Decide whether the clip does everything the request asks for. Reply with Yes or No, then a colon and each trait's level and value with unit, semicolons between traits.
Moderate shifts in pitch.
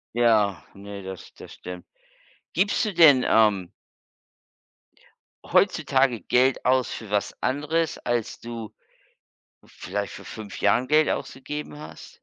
No: wide, 5.7 semitones